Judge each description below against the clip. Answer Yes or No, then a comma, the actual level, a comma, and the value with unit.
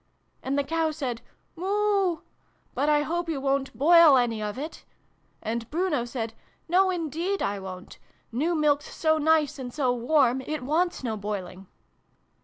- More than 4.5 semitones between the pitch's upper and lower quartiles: Yes, average, 5.3 semitones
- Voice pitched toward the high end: Yes, very high, 290 Hz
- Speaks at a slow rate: No, average, 170 wpm